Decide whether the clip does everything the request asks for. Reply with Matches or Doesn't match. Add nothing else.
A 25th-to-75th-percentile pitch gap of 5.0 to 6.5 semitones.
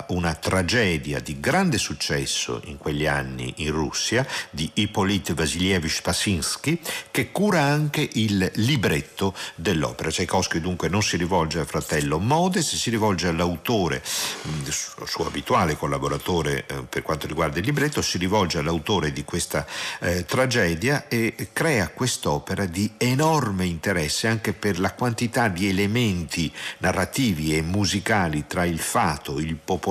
Matches